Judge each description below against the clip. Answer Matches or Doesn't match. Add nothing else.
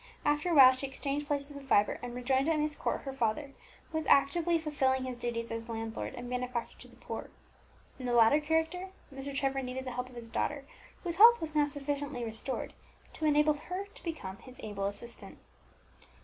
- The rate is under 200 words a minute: Doesn't match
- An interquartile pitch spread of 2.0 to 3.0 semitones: Doesn't match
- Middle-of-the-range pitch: Doesn't match